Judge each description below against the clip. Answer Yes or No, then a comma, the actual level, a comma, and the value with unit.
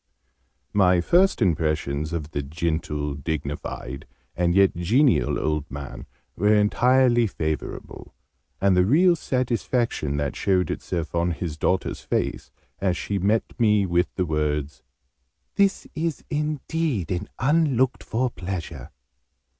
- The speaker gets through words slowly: Yes, slow, 120 wpm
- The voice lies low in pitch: Yes, very low, 90 Hz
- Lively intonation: Yes, wide, 7.6 semitones